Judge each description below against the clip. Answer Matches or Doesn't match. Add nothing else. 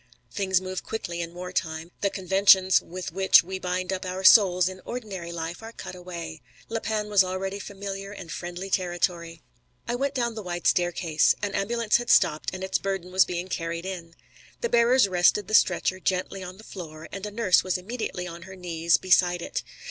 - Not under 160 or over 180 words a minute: Doesn't match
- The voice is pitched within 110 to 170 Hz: Doesn't match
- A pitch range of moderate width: Doesn't match